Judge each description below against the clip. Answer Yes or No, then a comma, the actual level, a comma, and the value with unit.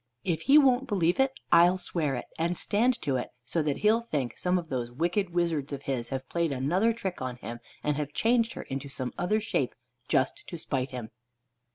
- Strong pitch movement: Yes, wide, 6.2 semitones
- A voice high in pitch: No, medium, 165 Hz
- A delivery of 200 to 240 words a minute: Yes, fast, 205 wpm